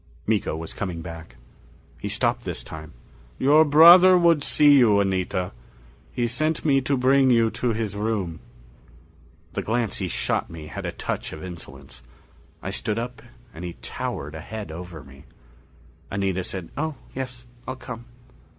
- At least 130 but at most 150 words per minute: No, average, 160 wpm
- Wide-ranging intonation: Yes, wide, 6.7 semitones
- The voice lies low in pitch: Yes, low, 110 Hz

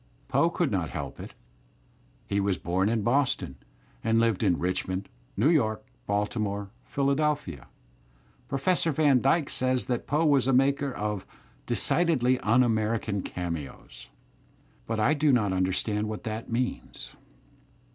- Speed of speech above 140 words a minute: No, slow, 135 wpm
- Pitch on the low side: Yes, low, 115 Hz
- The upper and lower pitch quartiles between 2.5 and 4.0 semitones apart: No, average, 5.2 semitones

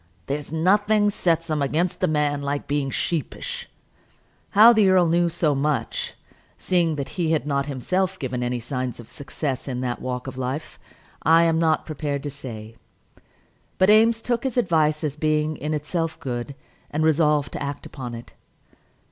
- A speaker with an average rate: Yes, average, 170 wpm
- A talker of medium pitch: Yes, medium, 150 Hz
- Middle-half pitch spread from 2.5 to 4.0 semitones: Yes, average, 3.6 semitones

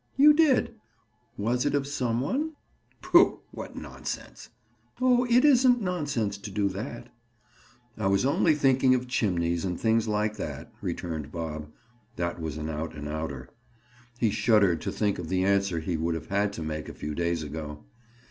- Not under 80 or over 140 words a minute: No, average, 170 wpm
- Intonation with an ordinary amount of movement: No, wide, 8.4 semitones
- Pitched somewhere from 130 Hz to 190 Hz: No, low, 100 Hz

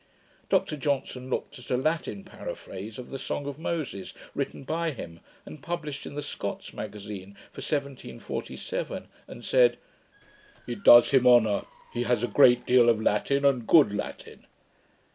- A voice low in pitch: Yes, low, 130 Hz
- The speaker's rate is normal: Yes, average, 155 wpm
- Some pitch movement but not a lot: Yes, average, 4.9 semitones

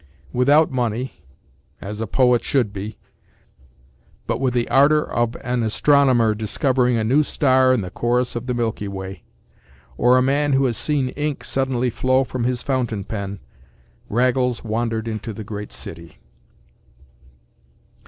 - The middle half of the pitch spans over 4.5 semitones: No, average, 3.3 semitones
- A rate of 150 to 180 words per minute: No, average, 140 wpm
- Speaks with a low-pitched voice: Yes, low, 120 Hz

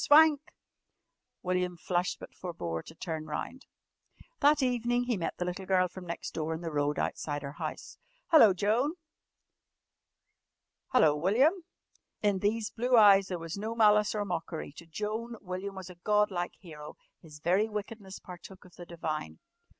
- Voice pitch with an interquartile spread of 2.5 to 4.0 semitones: No, average, 4.4 semitones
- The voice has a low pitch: No, medium, 185 Hz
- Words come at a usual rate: Yes, average, 160 wpm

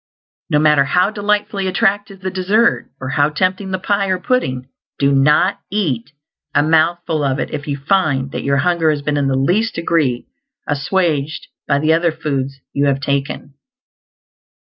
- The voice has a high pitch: No, medium, 155 Hz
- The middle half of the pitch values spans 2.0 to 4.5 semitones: No, average, 5.1 semitones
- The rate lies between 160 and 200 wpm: Yes, average, 165 wpm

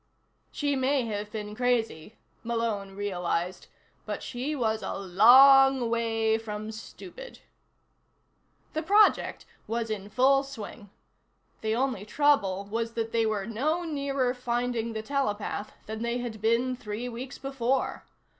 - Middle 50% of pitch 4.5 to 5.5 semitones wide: No, average, 3.6 semitones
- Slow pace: Yes, slow, 130 wpm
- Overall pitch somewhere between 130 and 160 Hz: No, high, 230 Hz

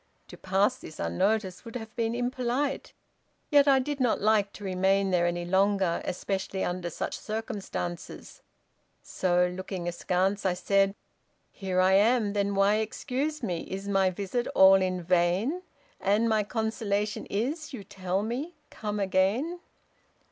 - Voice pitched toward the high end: Yes, high, 200 Hz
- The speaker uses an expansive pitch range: No, average, 3.5 semitones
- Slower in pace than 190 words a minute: Yes, average, 145 wpm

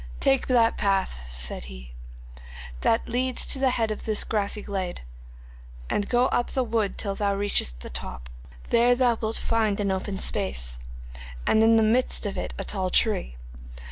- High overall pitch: Yes, high, 210 Hz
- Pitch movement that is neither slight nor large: Yes, average, 3.6 semitones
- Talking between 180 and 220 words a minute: No, average, 170 wpm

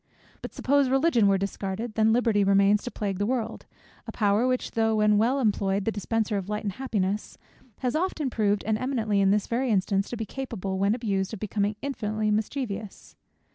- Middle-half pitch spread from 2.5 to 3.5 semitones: Yes, average, 3.2 semitones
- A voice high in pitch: Yes, high, 215 Hz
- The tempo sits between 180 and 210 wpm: Yes, average, 195 wpm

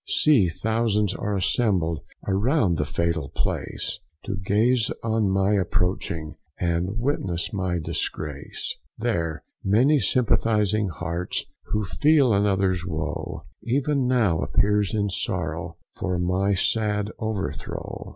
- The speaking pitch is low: Yes, low, 100 Hz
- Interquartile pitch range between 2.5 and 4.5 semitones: Yes, average, 4.0 semitones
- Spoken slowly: Yes, slow, 110 wpm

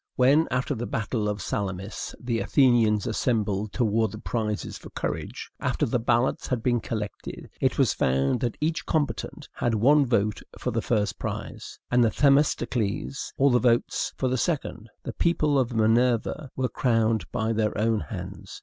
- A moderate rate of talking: Yes, average, 170 wpm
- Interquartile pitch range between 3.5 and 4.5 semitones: No, average, 3.0 semitones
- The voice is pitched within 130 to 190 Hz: No, low, 115 Hz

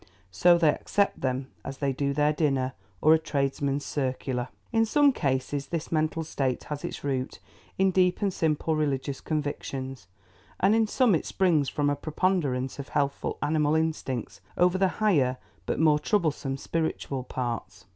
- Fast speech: No, average, 160 wpm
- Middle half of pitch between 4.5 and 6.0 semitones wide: No, average, 3.6 semitones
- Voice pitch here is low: No, medium, 145 Hz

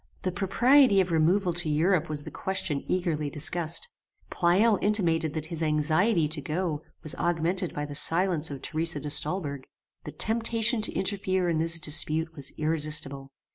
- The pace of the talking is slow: No, average, 160 wpm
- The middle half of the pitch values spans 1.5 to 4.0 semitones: Yes, average, 3.6 semitones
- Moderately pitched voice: Yes, medium, 165 Hz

